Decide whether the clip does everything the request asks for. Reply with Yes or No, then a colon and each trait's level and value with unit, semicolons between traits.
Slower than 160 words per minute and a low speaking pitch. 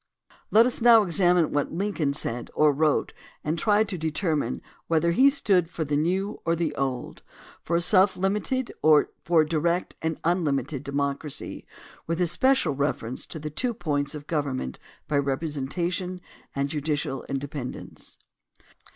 No: average, 150 wpm; medium, 160 Hz